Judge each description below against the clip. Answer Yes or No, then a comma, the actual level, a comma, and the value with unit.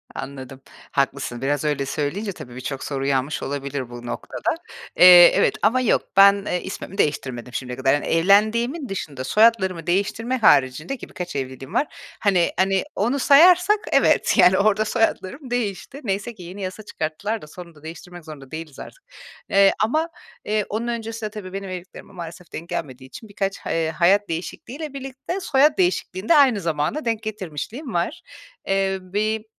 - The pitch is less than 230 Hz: Yes, high, 190 Hz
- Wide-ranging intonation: Yes, wide, 6.7 semitones